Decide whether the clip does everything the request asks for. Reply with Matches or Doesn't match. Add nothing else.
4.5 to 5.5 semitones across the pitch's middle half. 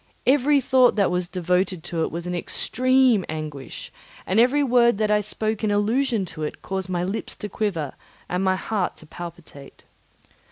Matches